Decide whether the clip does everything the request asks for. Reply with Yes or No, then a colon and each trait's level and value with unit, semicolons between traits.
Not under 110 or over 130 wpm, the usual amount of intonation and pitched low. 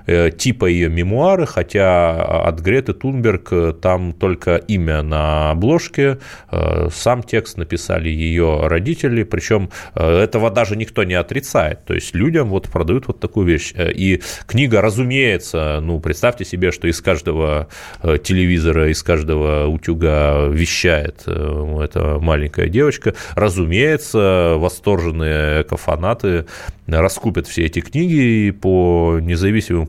Yes: average, 115 wpm; average, 5.0 semitones; very low, 90 Hz